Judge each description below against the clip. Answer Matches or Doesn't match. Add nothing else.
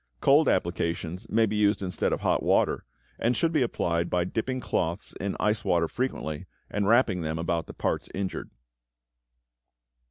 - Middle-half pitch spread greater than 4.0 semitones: Matches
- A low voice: Matches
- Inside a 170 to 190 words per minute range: Doesn't match